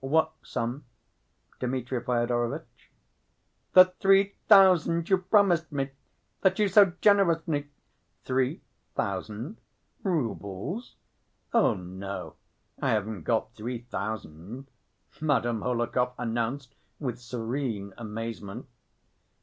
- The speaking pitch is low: Yes, low, 125 Hz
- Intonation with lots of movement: Yes, wide, 6.8 semitones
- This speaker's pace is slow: Yes, slow, 95 wpm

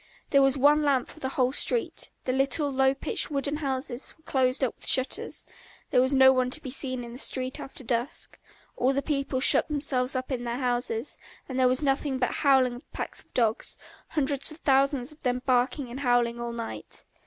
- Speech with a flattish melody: Yes, narrow, 1.9 semitones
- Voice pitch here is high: Yes, very high, 265 Hz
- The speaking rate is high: Yes, fast, 210 wpm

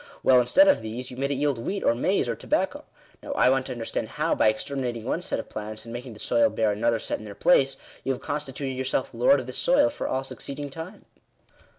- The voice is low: Yes, low, 130 Hz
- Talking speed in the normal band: No, fast, 240 wpm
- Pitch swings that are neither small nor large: Yes, average, 3.4 semitones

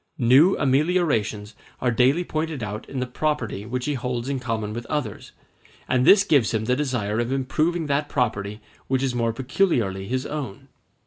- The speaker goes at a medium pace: Yes, average, 175 wpm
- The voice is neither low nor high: No, low, 125 Hz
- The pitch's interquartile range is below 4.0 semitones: No, average, 4.7 semitones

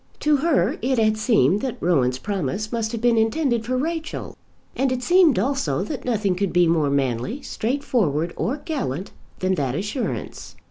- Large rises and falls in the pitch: Yes, wide, 7.1 semitones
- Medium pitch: No, high, 220 Hz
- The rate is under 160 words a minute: No, average, 170 wpm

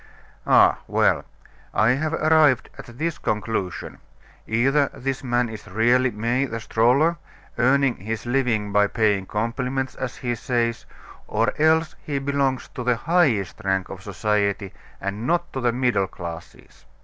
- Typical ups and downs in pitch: Yes, average, 4.3 semitones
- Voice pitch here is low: Yes, low, 120 Hz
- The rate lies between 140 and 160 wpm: Yes, average, 145 wpm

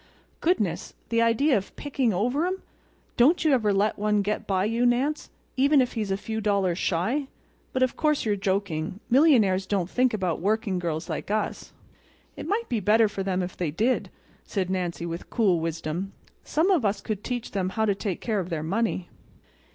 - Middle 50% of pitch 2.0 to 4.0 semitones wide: No, average, 4.7 semitones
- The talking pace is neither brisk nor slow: Yes, average, 185 wpm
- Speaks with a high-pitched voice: Yes, high, 210 Hz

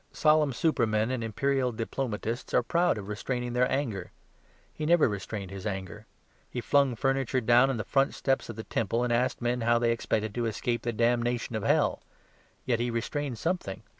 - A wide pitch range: No, average, 3.2 semitones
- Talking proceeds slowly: No, average, 180 wpm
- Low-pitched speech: Yes, low, 120 Hz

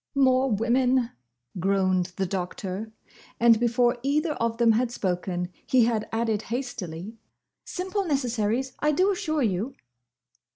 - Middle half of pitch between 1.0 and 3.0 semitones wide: No, average, 4.4 semitones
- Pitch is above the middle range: Yes, high, 235 Hz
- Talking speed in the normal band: No, slow, 125 wpm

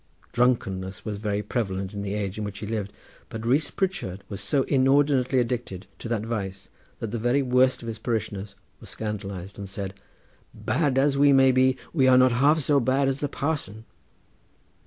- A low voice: Yes, low, 115 Hz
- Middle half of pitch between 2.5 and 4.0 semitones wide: No, average, 4.7 semitones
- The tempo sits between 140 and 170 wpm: No, average, 185 wpm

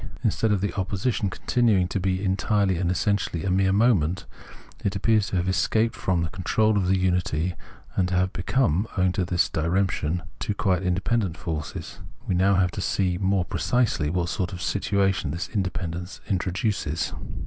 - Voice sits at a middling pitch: No, very low, 95 Hz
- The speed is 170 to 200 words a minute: Yes, average, 180 wpm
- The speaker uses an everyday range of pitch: No, narrow, 2.1 semitones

